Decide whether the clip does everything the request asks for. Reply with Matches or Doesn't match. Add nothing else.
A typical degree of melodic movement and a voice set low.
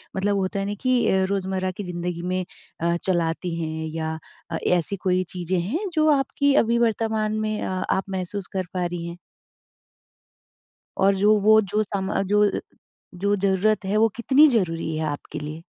Doesn't match